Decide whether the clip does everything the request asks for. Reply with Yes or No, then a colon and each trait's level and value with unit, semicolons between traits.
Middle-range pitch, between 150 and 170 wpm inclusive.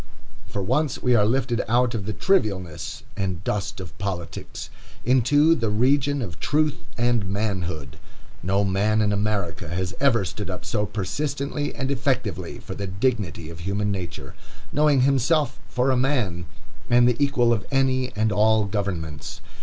No: low, 110 Hz; average, 155 wpm